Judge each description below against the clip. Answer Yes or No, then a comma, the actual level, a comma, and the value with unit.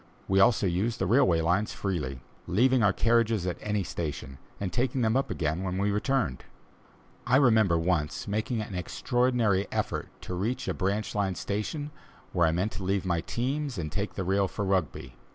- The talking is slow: No, average, 185 wpm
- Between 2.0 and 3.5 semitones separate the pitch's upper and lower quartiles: No, average, 4.4 semitones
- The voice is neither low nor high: No, low, 100 Hz